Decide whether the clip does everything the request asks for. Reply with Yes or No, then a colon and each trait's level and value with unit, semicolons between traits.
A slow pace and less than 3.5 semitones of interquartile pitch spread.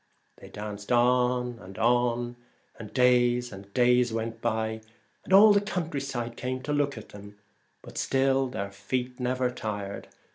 No: average, 155 wpm; narrow, 2.6 semitones